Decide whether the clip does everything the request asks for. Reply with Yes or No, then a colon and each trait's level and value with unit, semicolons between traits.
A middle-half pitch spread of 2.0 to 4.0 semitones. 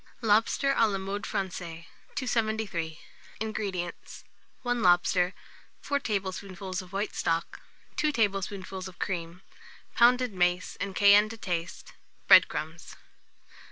Yes: average, 3.5 semitones